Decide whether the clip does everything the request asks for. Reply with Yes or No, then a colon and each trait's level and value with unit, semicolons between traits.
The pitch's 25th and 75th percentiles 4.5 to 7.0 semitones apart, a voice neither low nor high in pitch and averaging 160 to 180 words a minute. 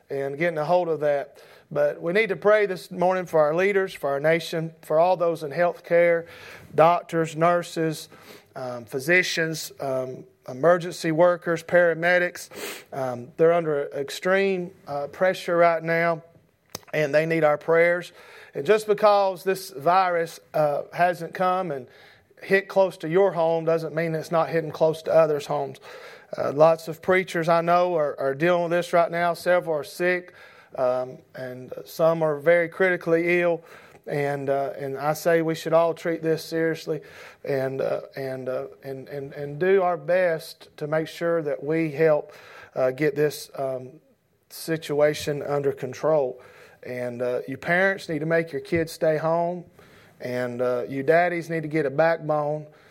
No: average, 3.0 semitones; medium, 165 Hz; average, 165 wpm